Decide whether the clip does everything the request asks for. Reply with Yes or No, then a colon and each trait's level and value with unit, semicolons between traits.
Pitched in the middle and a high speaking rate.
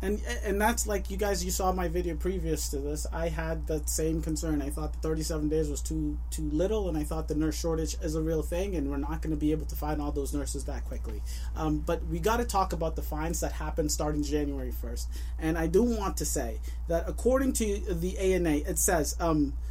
Yes: medium, 160 Hz; fast, 240 wpm